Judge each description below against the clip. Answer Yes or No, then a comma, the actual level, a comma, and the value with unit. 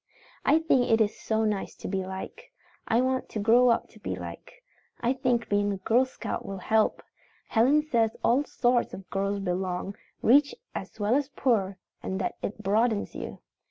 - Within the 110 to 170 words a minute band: No, average, 185 wpm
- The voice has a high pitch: Yes, high, 225 Hz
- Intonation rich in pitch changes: No, average, 4.0 semitones